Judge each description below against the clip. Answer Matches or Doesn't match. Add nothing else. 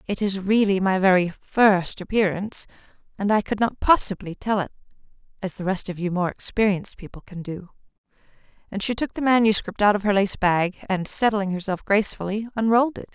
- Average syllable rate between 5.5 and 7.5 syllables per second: Matches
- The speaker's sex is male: Doesn't match